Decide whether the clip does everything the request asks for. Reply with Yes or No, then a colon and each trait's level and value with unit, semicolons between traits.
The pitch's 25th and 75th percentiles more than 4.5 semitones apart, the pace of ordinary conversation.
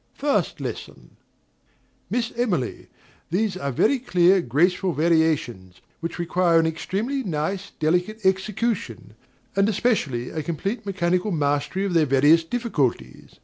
No: average, 4.9 semitones; slow, 120 wpm